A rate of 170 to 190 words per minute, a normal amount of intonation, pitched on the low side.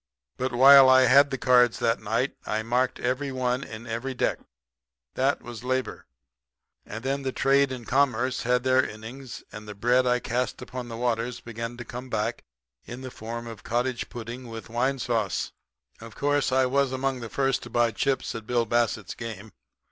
No: average, 185 wpm; narrow, 2.1 semitones; low, 125 Hz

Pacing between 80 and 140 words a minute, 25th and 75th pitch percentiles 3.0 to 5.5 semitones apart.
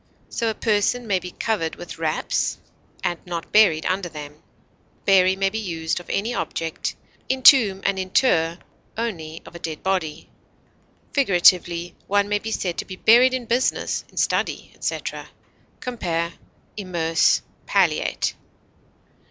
Yes: slow, 135 wpm; average, 4.6 semitones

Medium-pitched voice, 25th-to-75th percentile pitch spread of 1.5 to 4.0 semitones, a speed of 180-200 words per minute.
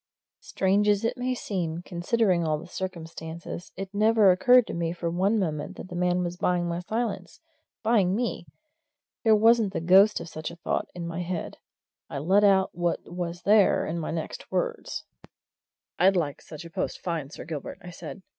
Yes: medium, 180 Hz; average, 3.3 semitones; average, 185 wpm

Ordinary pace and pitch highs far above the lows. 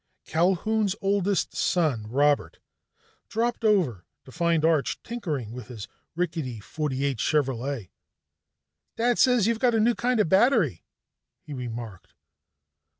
No: slow, 120 wpm; wide, 8.8 semitones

